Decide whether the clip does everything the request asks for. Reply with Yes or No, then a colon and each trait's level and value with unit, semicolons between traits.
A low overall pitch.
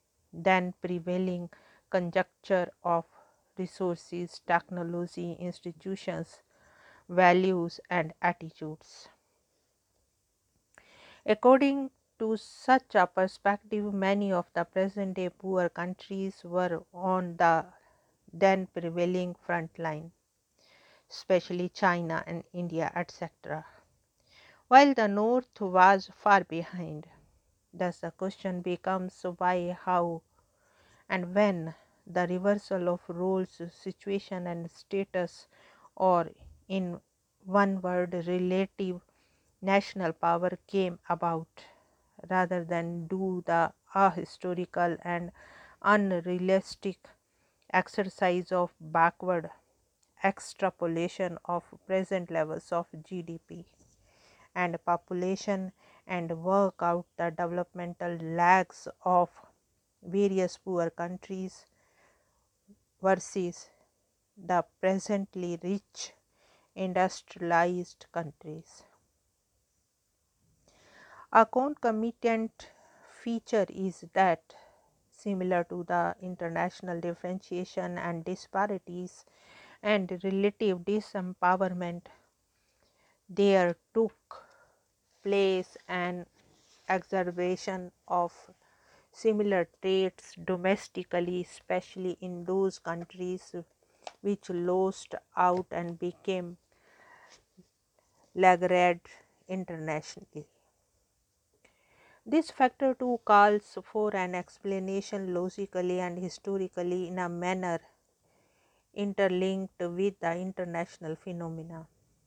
No: medium, 180 Hz